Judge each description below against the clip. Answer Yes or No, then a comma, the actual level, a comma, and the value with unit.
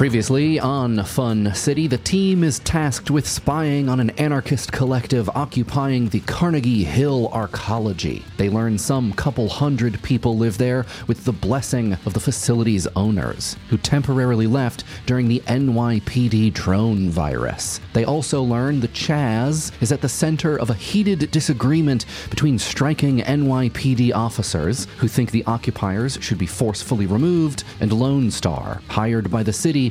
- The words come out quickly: No, average, 150 wpm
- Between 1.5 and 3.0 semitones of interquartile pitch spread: No, average, 4.1 semitones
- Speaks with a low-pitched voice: Yes, low, 120 Hz